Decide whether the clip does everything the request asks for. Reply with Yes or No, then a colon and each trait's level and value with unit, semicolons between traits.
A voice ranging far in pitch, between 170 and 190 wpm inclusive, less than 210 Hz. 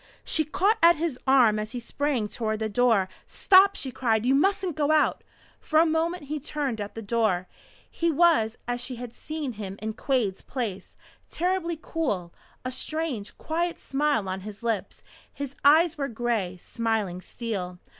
No: wide, 6.3 semitones; average, 175 wpm; very high, 250 Hz